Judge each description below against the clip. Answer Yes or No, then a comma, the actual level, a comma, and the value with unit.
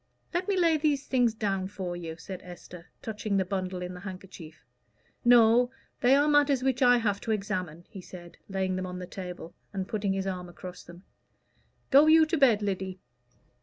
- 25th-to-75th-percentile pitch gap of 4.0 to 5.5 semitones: Yes, average, 5.2 semitones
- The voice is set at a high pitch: Yes, high, 195 Hz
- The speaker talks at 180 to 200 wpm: Yes, average, 190 wpm